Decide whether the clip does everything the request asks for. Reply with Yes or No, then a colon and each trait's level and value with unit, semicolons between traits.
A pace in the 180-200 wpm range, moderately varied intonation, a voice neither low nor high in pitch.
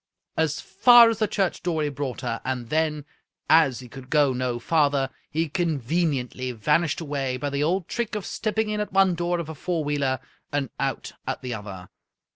Yes: average, 195 wpm; average, 5.0 semitones; medium, 150 Hz